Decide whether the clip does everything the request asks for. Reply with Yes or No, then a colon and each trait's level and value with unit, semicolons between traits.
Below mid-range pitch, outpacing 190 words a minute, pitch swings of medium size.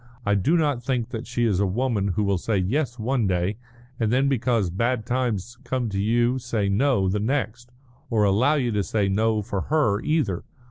Yes: low, 115 Hz; average, 200 wpm; average, 4.0 semitones